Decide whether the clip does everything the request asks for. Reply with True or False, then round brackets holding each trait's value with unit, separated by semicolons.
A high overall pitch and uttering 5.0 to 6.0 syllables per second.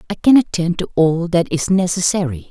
False (170 Hz; 5.4 syllables/s)